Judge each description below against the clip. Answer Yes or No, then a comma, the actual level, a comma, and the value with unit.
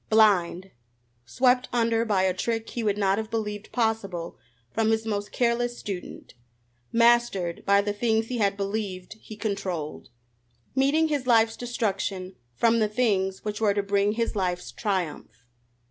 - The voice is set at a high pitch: Yes, high, 210 Hz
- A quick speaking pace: No, average, 150 wpm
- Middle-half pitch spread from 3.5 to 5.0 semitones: No, average, 3.0 semitones